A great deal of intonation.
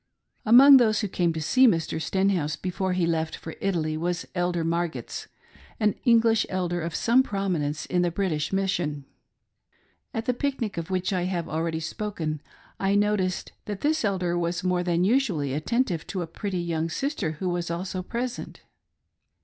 No: average, 3.8 semitones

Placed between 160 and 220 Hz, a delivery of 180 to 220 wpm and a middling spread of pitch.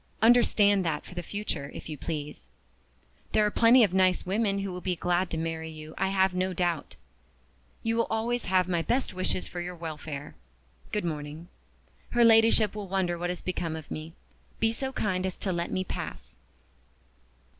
Yes: medium, 185 Hz; average, 185 wpm; average, 4.0 semitones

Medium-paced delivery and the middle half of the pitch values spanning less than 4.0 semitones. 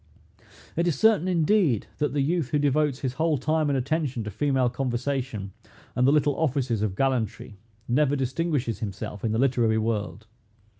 No: average, 165 wpm; average, 4.3 semitones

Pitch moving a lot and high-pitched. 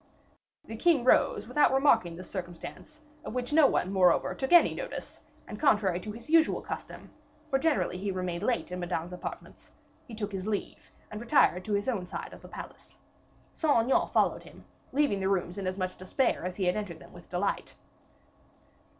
Yes: wide, 6.4 semitones; high, 205 Hz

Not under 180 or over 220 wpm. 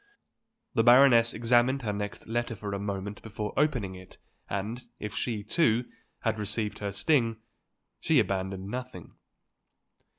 No: slow, 135 wpm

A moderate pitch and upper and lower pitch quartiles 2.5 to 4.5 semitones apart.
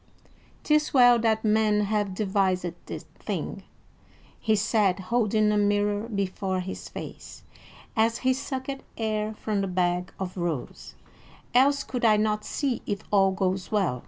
No: high, 210 Hz; average, 2.8 semitones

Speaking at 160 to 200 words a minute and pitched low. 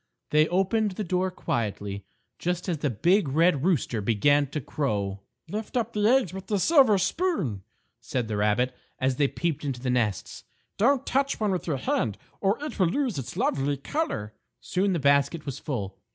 No: average, 180 wpm; medium, 155 Hz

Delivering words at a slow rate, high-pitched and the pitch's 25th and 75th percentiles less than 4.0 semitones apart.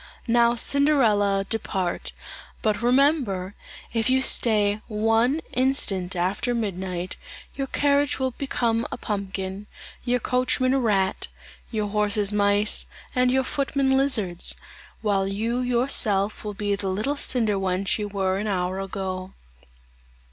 No: slow, 125 wpm; high, 210 Hz; average, 4.4 semitones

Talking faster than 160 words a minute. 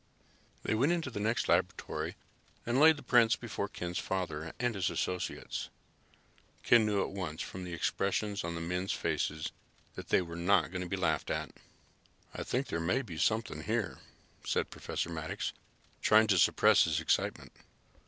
Yes: average, 170 wpm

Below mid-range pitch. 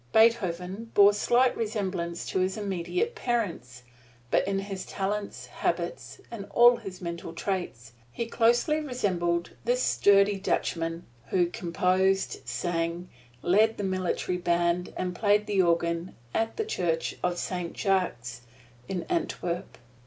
No: high, 190 Hz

